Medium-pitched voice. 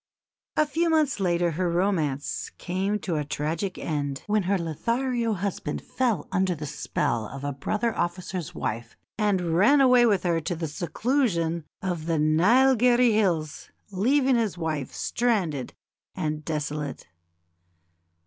Yes: medium, 180 Hz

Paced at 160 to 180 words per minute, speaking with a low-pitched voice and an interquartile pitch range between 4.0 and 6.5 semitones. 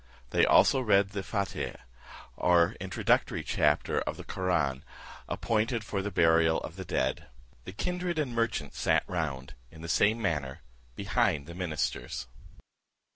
No: average, 140 wpm; very low, 95 Hz; average, 5.1 semitones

